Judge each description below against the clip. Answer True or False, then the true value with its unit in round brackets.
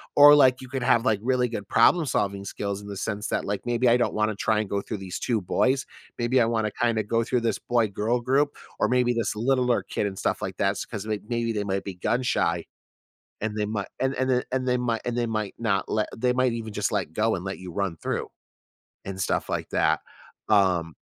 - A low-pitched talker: True (110 Hz)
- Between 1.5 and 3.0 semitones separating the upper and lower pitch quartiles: False (3.5 semitones)